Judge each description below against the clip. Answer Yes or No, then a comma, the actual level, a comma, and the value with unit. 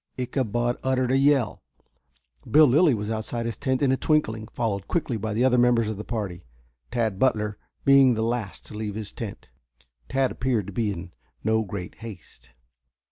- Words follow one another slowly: No, average, 180 wpm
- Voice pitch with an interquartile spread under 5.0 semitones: Yes, average, 3.5 semitones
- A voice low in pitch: Yes, low, 115 Hz